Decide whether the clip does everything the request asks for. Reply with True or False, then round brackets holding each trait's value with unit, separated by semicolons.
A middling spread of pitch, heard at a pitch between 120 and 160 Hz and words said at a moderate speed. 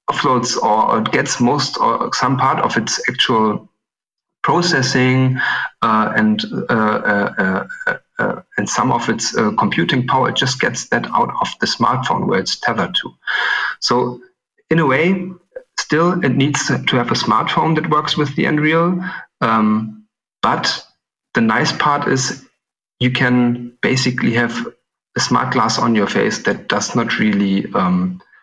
False (6.9 semitones; 140 Hz; 155 wpm)